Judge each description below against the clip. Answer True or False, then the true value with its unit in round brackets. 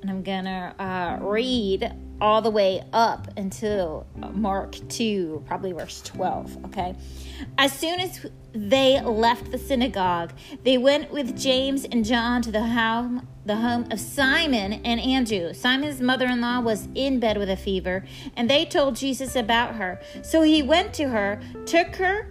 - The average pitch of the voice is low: False (235 Hz)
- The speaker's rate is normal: True (160 wpm)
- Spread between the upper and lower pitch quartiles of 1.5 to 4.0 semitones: False (5.3 semitones)